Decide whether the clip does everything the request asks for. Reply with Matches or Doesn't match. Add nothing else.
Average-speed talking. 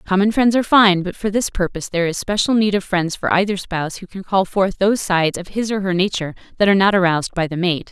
Doesn't match